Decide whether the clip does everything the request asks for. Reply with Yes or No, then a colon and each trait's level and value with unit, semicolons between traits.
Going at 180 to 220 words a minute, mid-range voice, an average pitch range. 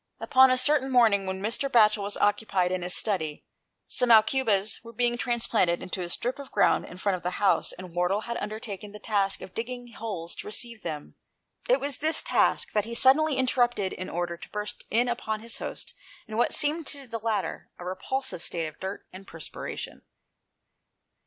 No: average, 190 wpm; high, 215 Hz; average, 4.4 semitones